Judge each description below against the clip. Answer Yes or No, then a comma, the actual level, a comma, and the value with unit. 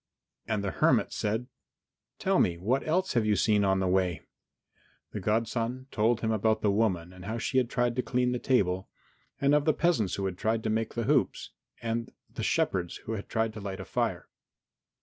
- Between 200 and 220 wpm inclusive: Yes, fast, 205 wpm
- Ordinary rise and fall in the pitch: Yes, average, 3.6 semitones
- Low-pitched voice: Yes, low, 110 Hz